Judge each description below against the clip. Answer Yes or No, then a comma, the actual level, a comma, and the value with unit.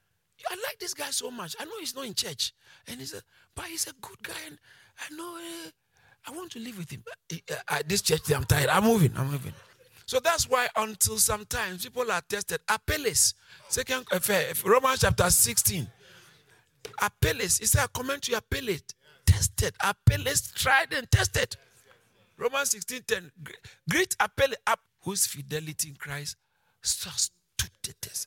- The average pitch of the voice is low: No, high, 220 Hz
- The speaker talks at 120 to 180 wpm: Yes, average, 170 wpm